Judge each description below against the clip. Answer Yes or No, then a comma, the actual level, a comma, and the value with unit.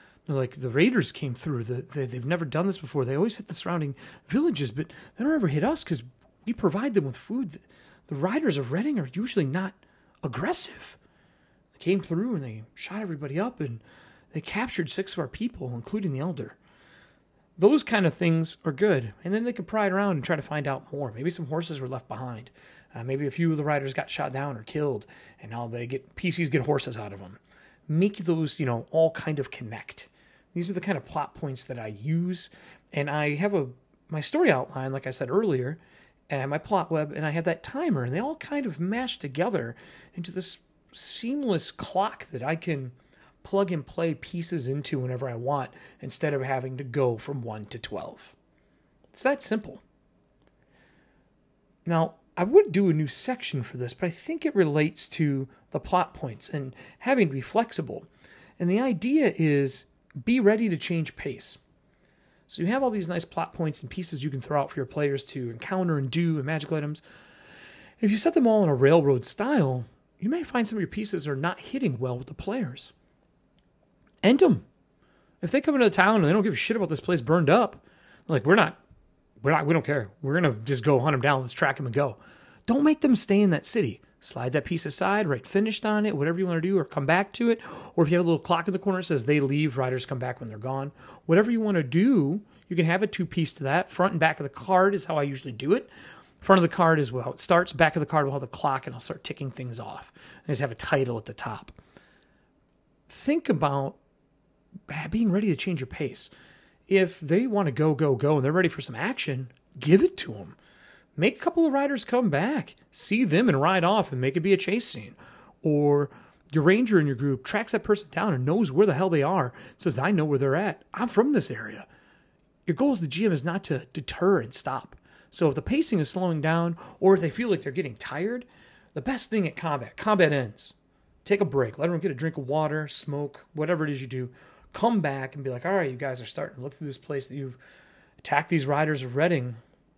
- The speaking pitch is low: No, medium, 160 Hz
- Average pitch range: No, wide, 6.0 semitones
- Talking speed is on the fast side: Yes, fast, 230 wpm